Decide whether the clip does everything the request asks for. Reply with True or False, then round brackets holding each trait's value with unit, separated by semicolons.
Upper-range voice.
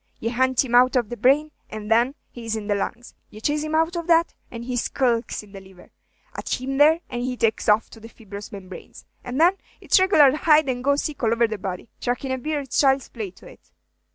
True (245 Hz)